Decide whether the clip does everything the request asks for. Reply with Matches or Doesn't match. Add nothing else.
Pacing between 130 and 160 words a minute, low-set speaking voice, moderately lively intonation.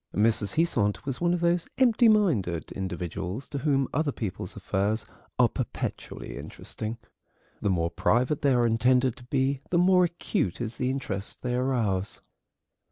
Doesn't match